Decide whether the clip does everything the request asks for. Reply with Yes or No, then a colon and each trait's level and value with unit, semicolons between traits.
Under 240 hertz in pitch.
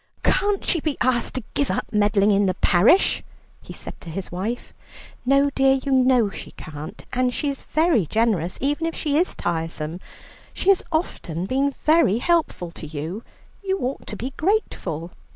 No: high, 245 Hz